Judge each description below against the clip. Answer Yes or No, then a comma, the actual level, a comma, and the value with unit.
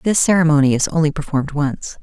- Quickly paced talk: No, average, 180 wpm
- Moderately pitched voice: Yes, medium, 155 Hz